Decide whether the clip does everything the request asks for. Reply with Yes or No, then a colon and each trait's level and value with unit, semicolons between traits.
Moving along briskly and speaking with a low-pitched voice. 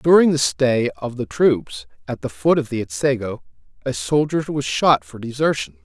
No: average, 185 wpm; low, 125 Hz